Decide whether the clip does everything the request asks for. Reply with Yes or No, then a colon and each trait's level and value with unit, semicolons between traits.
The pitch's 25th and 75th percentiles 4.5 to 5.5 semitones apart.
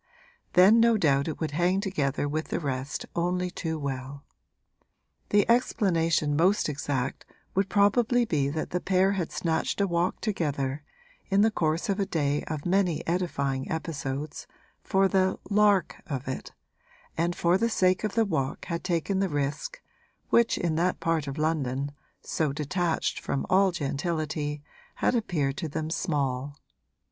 Yes: average, 4.9 semitones